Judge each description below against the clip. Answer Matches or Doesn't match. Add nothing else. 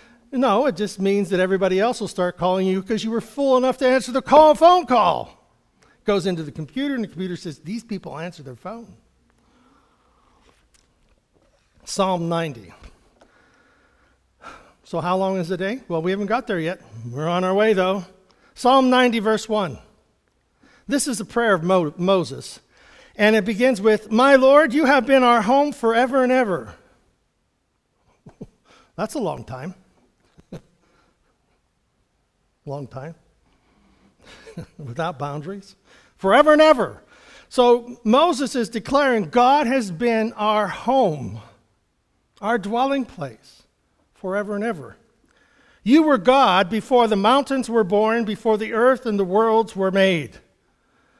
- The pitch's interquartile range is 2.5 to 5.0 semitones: Doesn't match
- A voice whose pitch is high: Matches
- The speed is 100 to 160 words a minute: Matches